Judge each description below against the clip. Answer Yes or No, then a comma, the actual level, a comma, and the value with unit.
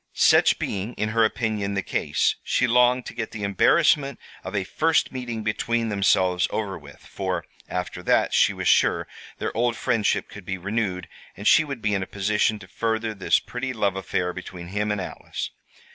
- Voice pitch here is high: No, low, 105 Hz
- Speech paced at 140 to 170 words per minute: No, average, 190 wpm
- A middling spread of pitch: Yes, average, 3.4 semitones